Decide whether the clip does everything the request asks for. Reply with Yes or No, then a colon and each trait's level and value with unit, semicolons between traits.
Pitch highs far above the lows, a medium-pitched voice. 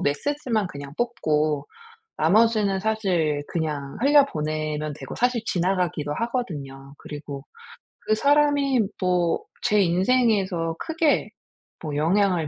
Yes: wide, 7.2 semitones; medium, 180 Hz